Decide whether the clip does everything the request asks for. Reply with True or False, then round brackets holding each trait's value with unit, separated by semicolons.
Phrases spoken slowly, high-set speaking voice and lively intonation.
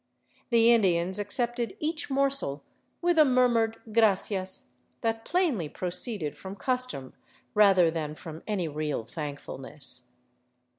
True (120 wpm; 205 Hz; 7.0 semitones)